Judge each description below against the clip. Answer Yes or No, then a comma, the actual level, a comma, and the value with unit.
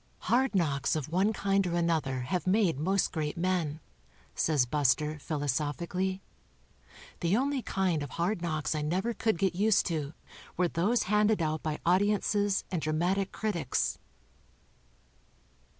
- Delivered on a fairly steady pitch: No, average, 4.3 semitones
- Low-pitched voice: No, medium, 175 Hz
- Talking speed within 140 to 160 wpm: Yes, average, 155 wpm